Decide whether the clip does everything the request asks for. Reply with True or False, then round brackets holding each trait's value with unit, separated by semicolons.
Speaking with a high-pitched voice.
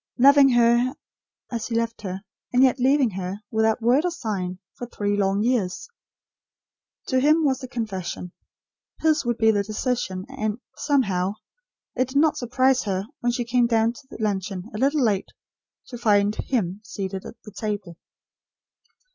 True (230 Hz)